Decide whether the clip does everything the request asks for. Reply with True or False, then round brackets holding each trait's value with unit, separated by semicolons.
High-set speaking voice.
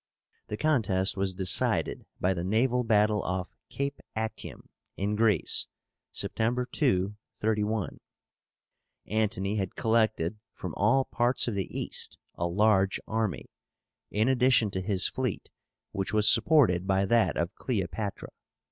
False (105 Hz)